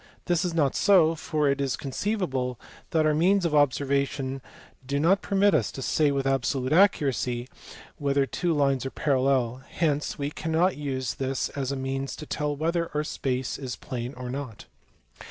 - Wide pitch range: No, average, 3.1 semitones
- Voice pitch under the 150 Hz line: Yes, medium, 140 Hz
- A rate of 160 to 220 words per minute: Yes, average, 170 wpm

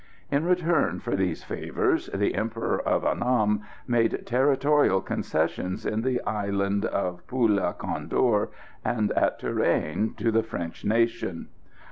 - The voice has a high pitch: No, low, 110 Hz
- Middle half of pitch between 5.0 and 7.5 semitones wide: No, average, 3.9 semitones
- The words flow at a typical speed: No, slow, 125 wpm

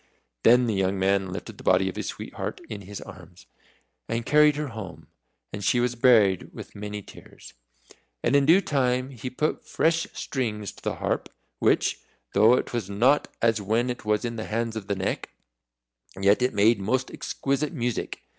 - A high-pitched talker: No, low, 115 Hz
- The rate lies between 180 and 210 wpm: Yes, average, 185 wpm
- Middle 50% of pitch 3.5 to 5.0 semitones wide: Yes, average, 4.1 semitones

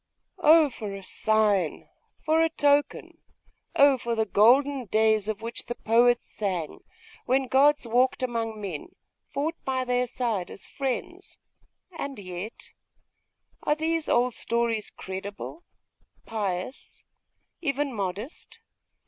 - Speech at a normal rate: No, slow, 120 wpm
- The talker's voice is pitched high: Yes, high, 235 Hz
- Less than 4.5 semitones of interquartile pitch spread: No, average, 4.9 semitones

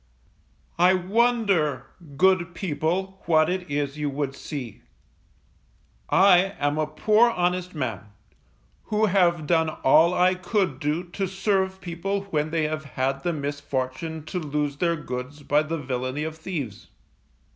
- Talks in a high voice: No, medium, 160 Hz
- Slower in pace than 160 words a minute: Yes, average, 140 wpm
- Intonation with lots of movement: No, average, 4.2 semitones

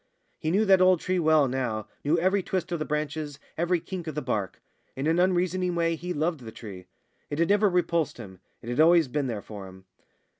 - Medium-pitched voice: Yes, medium, 160 Hz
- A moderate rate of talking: No, fast, 220 wpm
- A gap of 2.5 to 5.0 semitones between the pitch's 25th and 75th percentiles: No, wide, 5.5 semitones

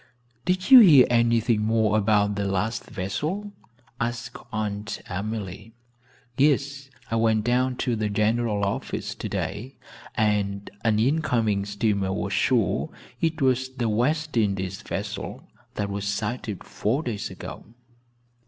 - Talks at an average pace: No, slow, 125 wpm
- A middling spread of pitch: Yes, average, 3.8 semitones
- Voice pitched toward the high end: No, low, 110 Hz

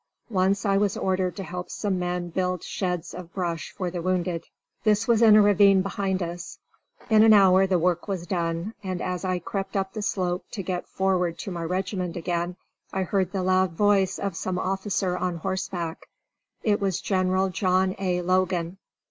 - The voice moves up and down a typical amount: No, narrow, 1.6 semitones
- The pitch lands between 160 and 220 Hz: Yes, medium, 185 Hz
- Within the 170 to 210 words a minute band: Yes, average, 185 wpm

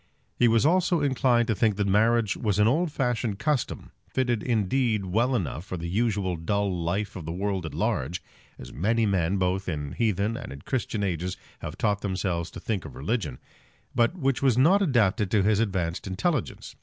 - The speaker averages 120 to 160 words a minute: No, average, 190 wpm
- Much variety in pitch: No, average, 4.5 semitones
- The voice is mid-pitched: No, low, 105 Hz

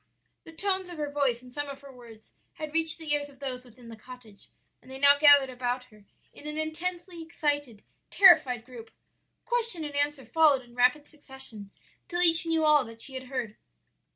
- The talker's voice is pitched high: Yes, very high, 285 Hz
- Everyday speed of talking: Yes, average, 195 wpm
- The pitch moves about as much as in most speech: Yes, average, 4.0 semitones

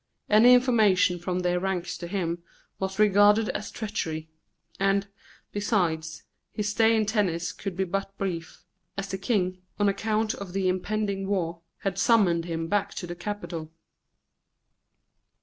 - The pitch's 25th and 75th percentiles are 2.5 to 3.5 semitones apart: Yes, average, 2.8 semitones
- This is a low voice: No, high, 195 Hz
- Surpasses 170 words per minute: No, average, 145 wpm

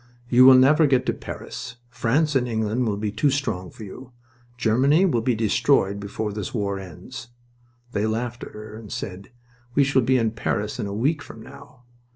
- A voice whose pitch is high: No, low, 115 Hz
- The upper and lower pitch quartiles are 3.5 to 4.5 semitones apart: Yes, average, 3.8 semitones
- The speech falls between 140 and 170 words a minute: No, average, 195 wpm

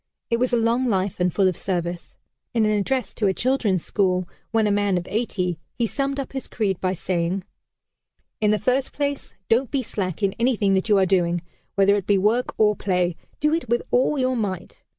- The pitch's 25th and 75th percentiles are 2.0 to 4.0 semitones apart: No, average, 4.5 semitones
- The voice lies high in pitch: Yes, high, 205 Hz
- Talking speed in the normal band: No, fast, 210 wpm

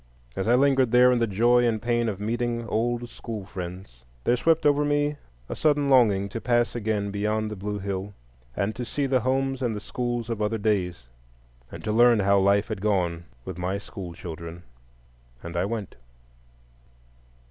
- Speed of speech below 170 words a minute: No, average, 180 wpm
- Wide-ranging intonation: No, average, 3.7 semitones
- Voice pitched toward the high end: No, low, 110 Hz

